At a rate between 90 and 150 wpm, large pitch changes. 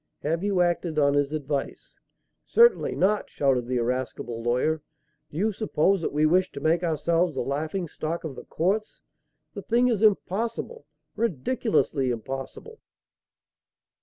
Yes: average, 140 wpm; wide, 6.0 semitones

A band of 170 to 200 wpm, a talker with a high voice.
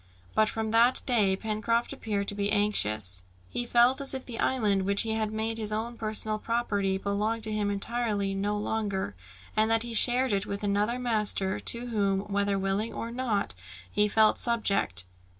Yes: average, 180 wpm; high, 215 Hz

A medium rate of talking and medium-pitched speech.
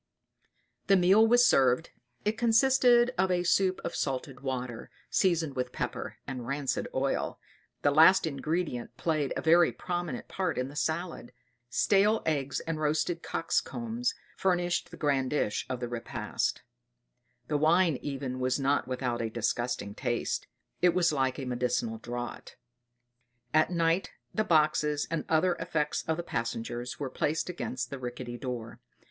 Yes: average, 150 wpm; medium, 150 Hz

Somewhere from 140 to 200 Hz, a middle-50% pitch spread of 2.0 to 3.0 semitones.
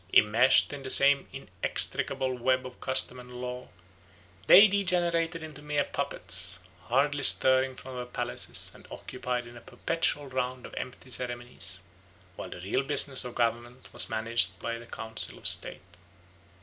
No: low, 125 Hz; average, 2.7 semitones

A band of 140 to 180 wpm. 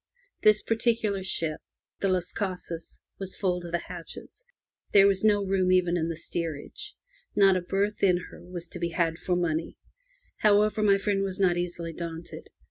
Yes: average, 175 wpm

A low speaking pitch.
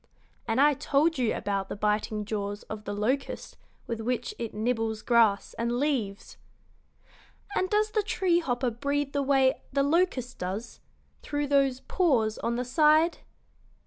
No: very high, 250 Hz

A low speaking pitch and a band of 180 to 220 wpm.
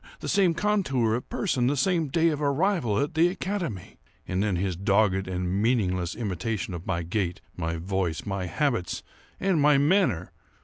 No: low, 110 Hz; average, 170 wpm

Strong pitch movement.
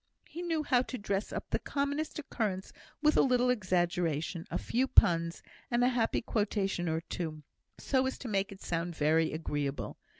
Yes: wide, 7.2 semitones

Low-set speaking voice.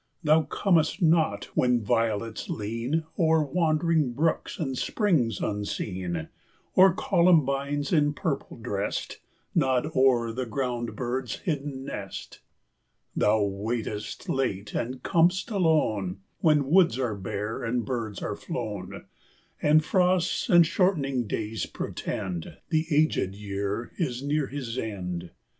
Yes: low, 130 Hz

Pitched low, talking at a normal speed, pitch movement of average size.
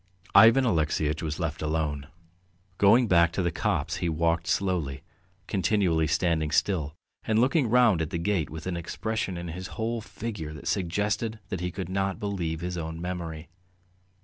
Yes: very low, 85 Hz; average, 165 wpm; average, 4.1 semitones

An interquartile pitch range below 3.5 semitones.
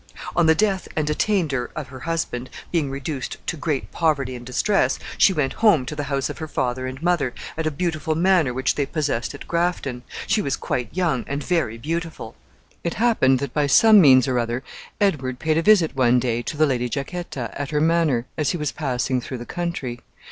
No: average, 4.5 semitones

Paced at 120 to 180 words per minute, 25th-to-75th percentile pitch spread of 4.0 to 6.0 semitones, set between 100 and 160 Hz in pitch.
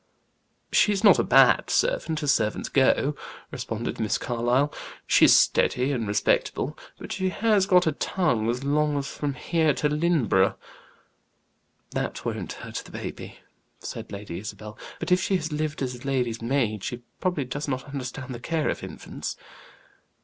Yes: average, 155 wpm; average, 4.8 semitones; medium, 140 Hz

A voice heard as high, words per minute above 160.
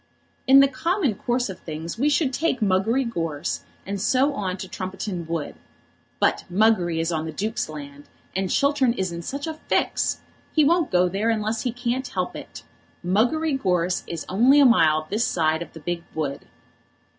Yes: high, 200 Hz; average, 180 wpm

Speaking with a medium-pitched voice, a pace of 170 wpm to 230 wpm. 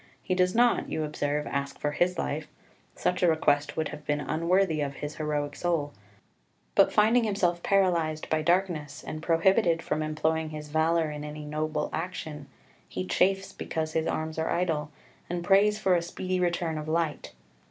Yes: medium, 160 Hz; average, 175 wpm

